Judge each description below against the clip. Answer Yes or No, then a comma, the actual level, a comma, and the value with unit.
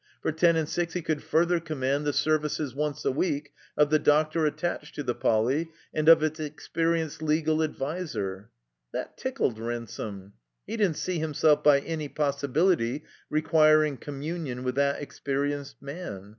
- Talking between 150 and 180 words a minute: Yes, average, 155 wpm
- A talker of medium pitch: Yes, medium, 150 Hz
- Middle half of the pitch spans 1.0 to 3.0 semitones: Yes, narrow, 2.4 semitones